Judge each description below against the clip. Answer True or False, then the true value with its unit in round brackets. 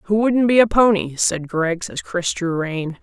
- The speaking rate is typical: False (220 wpm)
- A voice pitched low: False (190 Hz)